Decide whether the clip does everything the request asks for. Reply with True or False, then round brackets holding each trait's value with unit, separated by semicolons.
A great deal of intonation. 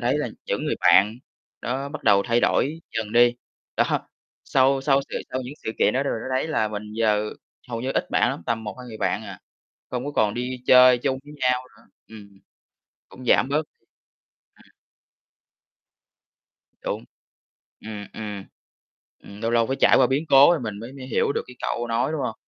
False (3.5 semitones)